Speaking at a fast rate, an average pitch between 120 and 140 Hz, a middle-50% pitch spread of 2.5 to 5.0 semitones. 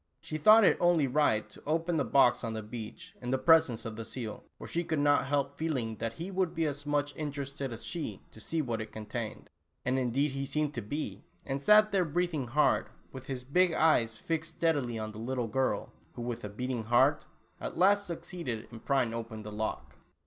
No: fast, 215 wpm; low, 135 Hz; wide, 5.6 semitones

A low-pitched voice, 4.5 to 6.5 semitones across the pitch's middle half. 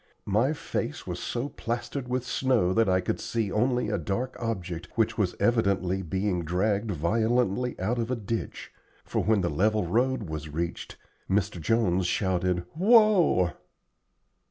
Yes: low, 105 Hz; average, 4.8 semitones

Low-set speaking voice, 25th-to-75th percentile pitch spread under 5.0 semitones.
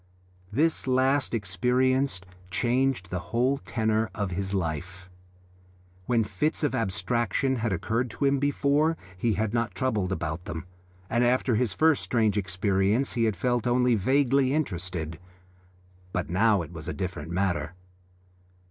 No: low, 110 Hz; wide, 5.6 semitones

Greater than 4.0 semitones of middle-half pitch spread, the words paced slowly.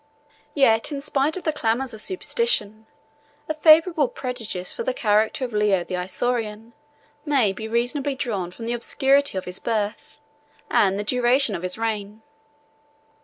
No: average, 4.7 semitones; average, 155 wpm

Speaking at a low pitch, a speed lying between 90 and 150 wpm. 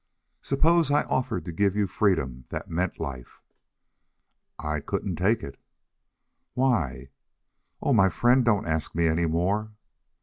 Yes: very low, 95 Hz; slow, 135 wpm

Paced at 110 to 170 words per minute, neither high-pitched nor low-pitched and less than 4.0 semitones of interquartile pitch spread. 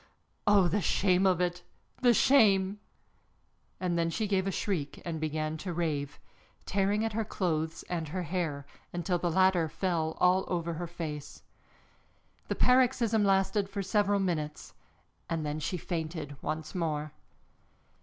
Yes: average, 145 wpm; medium, 175 Hz; average, 3.5 semitones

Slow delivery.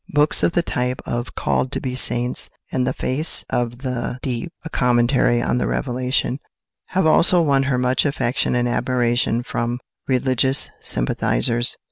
No: average, 155 wpm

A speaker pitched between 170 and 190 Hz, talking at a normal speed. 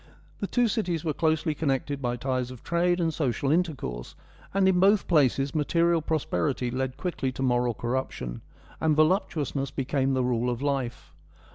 No: medium, 140 Hz; average, 160 wpm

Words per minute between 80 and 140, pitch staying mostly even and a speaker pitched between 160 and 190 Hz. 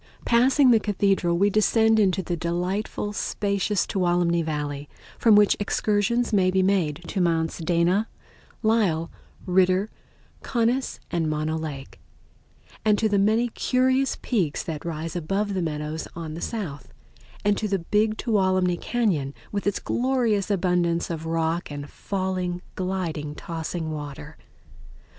No: slow, 135 wpm; average, 4.3 semitones; medium, 185 Hz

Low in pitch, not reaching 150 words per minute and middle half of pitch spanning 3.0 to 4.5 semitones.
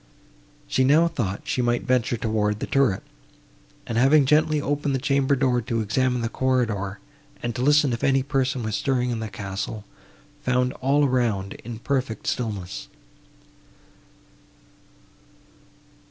Yes: low, 125 Hz; average, 140 wpm; average, 3.5 semitones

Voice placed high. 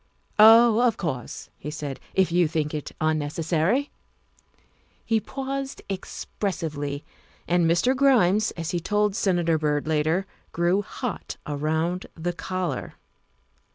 No: medium, 175 Hz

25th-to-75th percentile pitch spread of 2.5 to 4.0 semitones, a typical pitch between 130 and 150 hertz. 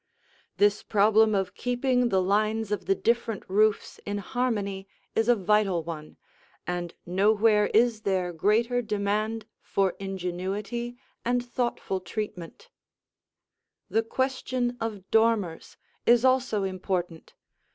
No: average, 3.5 semitones; high, 210 Hz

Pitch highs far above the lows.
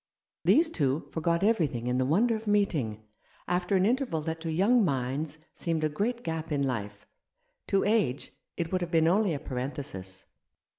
Yes: wide, 6.6 semitones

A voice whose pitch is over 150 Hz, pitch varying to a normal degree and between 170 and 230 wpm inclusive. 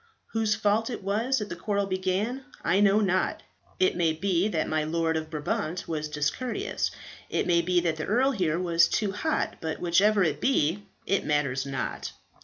Yes: medium, 185 Hz; average, 4.6 semitones; average, 185 wpm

